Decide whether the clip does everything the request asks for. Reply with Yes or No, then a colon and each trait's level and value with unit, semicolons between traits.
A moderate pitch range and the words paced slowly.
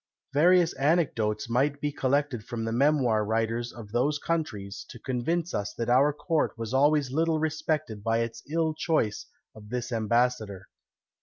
No: average, 5.0 semitones; average, 155 wpm